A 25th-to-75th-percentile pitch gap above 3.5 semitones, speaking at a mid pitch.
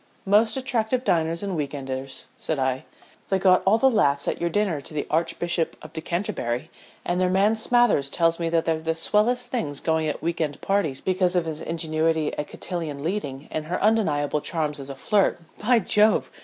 Yes: average, 5.0 semitones; medium, 165 Hz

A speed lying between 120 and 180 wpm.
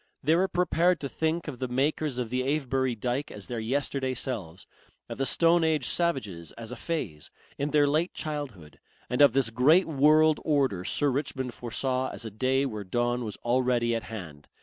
No: average, 190 wpm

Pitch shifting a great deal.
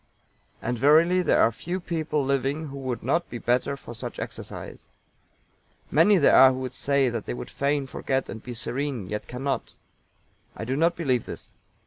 No: average, 3.7 semitones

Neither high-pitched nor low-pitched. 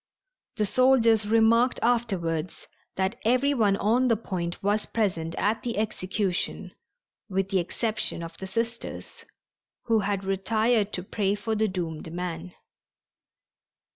No: high, 205 Hz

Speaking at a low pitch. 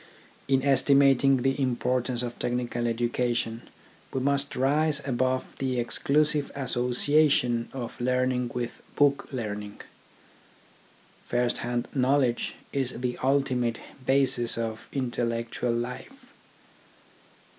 Yes: low, 125 Hz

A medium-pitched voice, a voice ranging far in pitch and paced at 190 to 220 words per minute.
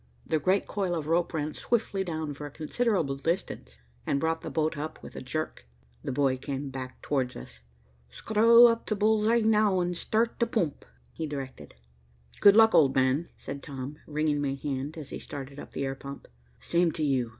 Yes: medium, 155 Hz; wide, 5.7 semitones; average, 195 wpm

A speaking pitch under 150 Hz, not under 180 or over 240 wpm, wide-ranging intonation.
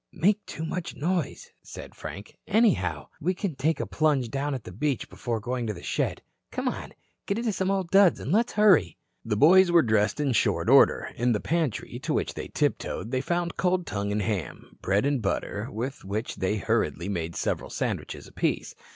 Yes: low, 135 Hz; average, 195 wpm; wide, 8.7 semitones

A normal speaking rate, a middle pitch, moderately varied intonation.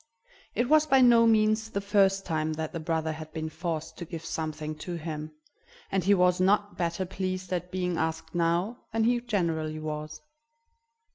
Yes: average, 180 wpm; medium, 175 Hz; average, 4.0 semitones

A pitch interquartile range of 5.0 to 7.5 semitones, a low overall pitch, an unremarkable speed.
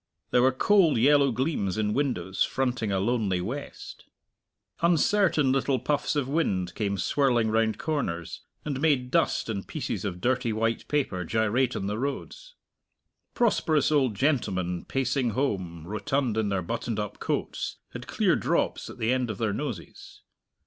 Yes: wide, 5.5 semitones; low, 120 Hz; average, 155 wpm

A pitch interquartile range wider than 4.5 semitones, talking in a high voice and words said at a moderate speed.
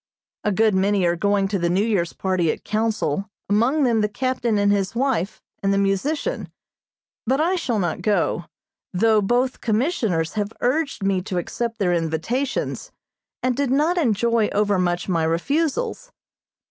Yes: average, 5.2 semitones; high, 210 Hz; average, 160 wpm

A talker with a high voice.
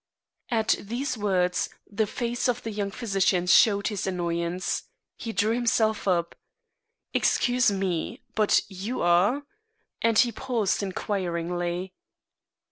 Yes: high, 200 Hz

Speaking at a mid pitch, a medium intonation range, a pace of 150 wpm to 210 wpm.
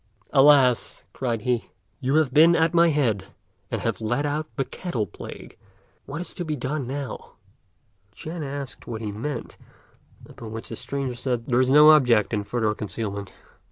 No: low, 130 Hz; average, 4.6 semitones; average, 170 wpm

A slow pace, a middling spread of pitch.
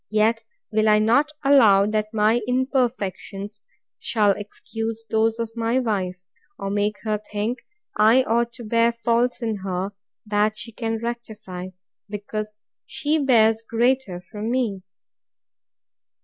No: slow, 130 wpm; narrow, 2.2 semitones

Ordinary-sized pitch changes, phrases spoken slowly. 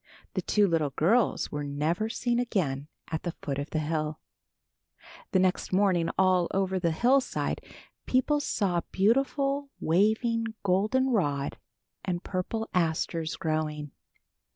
No: wide, 6.0 semitones; slow, 130 wpm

